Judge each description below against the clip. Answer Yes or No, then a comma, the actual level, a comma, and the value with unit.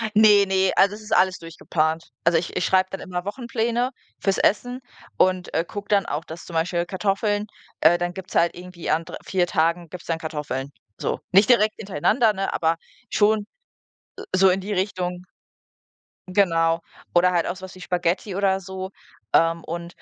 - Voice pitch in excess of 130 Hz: Yes, medium, 185 Hz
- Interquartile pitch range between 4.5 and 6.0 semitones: No, average, 2.9 semitones